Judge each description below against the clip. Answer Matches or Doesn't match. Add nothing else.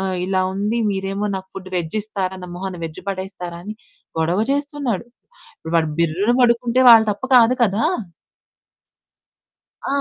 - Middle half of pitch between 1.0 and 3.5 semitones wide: Doesn't match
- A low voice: Doesn't match